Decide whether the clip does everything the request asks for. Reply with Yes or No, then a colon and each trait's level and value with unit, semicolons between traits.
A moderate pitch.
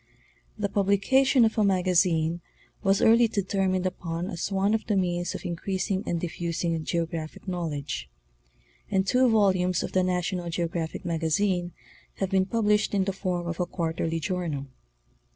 Yes: medium, 180 Hz